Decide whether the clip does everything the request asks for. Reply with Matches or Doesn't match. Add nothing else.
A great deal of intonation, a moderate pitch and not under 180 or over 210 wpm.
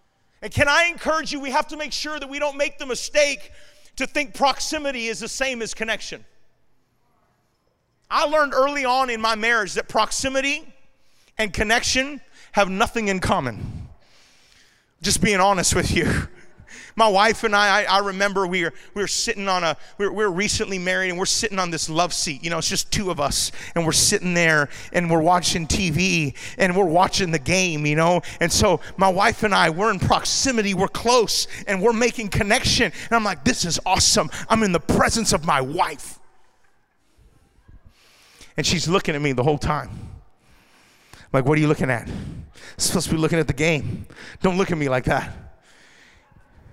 Doesn't match